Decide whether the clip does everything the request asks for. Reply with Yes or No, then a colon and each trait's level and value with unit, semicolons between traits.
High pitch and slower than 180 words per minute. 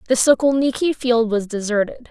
Yes: high, 240 Hz; average, 140 wpm